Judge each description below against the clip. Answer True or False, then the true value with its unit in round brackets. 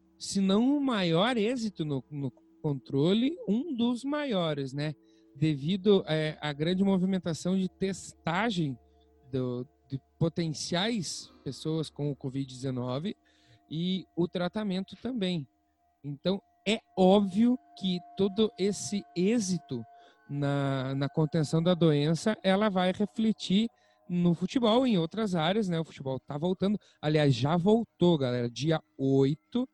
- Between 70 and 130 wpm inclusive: True (125 wpm)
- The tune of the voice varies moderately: False (5.7 semitones)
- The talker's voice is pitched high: False (175 Hz)